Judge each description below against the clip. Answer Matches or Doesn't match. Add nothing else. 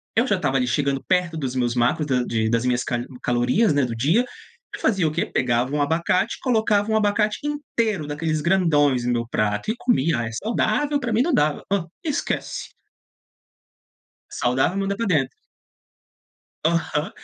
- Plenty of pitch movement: Matches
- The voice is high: Doesn't match